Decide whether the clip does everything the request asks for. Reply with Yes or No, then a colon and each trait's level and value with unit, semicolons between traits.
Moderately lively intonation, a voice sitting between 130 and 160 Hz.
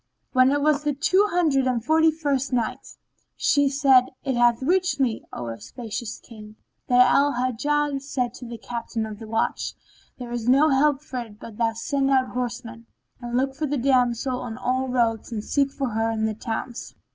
No: average, 3.2 semitones; very high, 255 Hz